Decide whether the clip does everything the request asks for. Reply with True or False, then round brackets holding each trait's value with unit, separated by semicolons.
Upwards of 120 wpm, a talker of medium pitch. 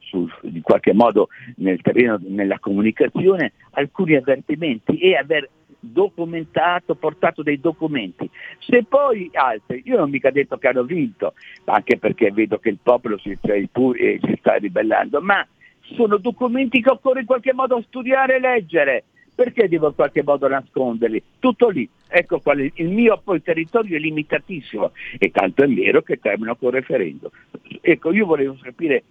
True (155 wpm; 165 Hz)